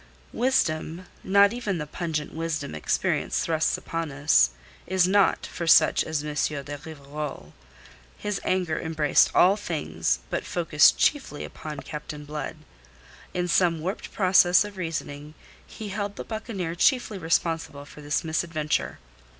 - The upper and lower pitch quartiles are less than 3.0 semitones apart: No, average, 3.9 semitones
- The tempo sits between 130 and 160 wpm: Yes, slow, 135 wpm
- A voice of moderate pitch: Yes, medium, 165 Hz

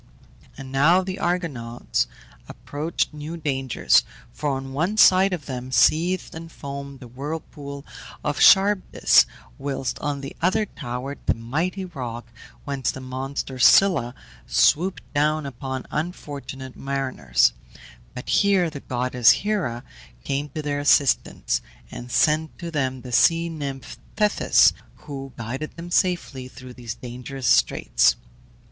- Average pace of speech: No, slow, 130 wpm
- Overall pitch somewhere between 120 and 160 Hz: Yes, medium, 140 Hz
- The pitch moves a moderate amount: Yes, average, 4.3 semitones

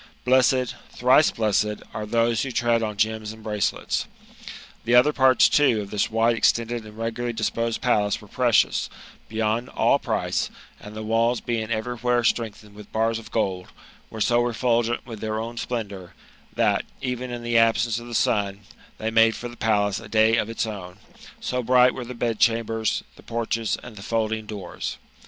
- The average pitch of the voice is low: Yes, low, 115 Hz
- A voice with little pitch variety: Yes, narrow, 1.8 semitones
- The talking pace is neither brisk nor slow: Yes, average, 180 wpm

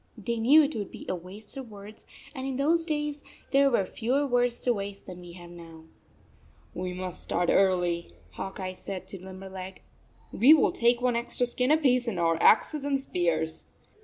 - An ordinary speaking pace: Yes, average, 190 wpm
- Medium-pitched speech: No, high, 210 Hz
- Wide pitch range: Yes, wide, 6.1 semitones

